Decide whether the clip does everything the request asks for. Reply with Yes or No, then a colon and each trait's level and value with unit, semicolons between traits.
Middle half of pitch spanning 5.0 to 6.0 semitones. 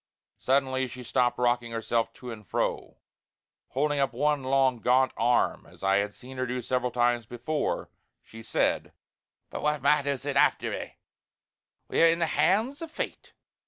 No: average, 2.8 semitones